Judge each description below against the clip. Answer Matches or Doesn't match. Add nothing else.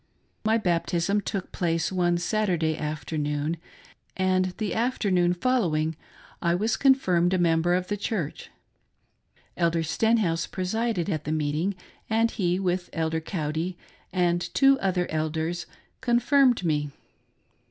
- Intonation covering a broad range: Doesn't match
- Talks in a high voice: Doesn't match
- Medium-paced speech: Doesn't match